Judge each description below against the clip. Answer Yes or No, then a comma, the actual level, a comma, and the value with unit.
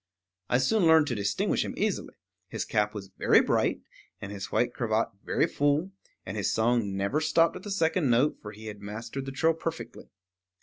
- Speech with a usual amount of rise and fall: No, wide, 7.3 semitones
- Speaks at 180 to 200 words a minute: Yes, average, 190 wpm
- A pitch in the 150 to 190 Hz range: No, low, 120 Hz